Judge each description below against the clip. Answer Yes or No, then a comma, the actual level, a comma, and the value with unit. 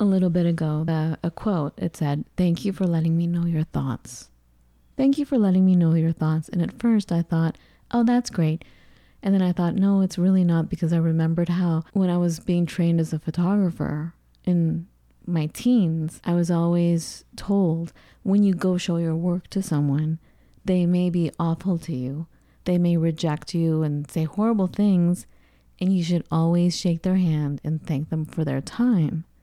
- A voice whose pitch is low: No, medium, 170 Hz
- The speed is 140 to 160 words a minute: No, average, 195 wpm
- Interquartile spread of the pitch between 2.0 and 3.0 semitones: Yes, narrow, 2.4 semitones